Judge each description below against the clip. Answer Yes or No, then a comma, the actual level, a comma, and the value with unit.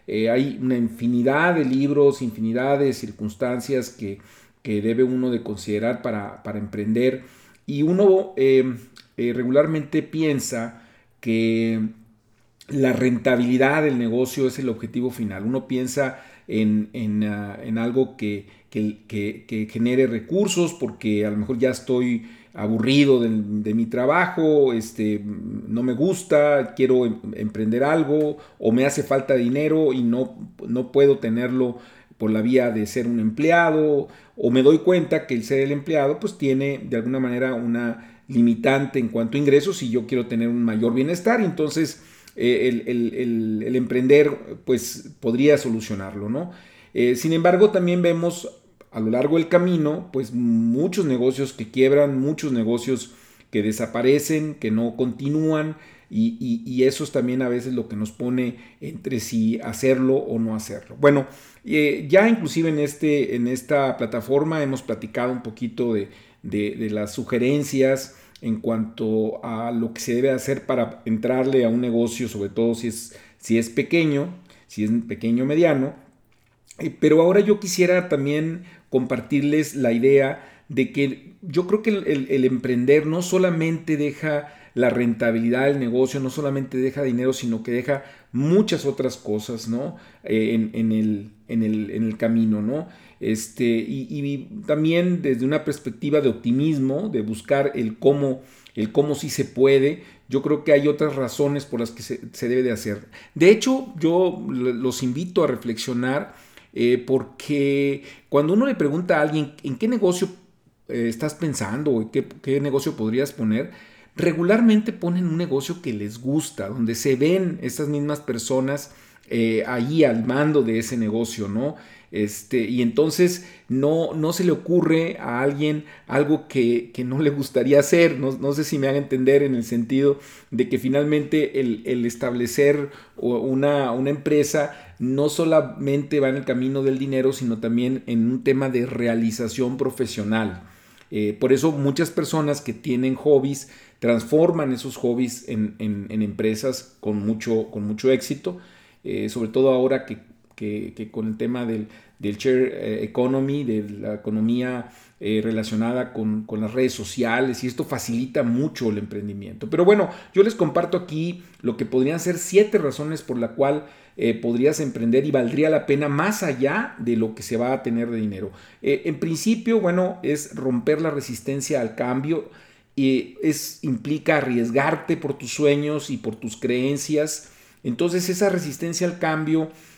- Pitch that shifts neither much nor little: Yes, average, 4.2 semitones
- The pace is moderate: Yes, average, 165 wpm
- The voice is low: Yes, low, 130 Hz